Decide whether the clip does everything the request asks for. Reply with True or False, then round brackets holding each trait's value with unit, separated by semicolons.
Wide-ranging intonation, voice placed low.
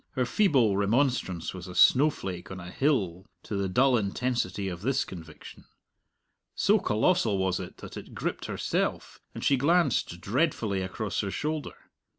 True (6.4 semitones; 105 Hz)